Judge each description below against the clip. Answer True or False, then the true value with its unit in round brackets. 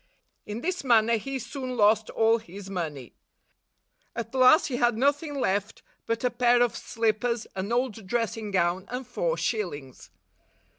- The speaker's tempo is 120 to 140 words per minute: False (155 wpm)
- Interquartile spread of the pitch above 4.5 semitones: False (3.4 semitones)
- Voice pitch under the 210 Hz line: False (230 Hz)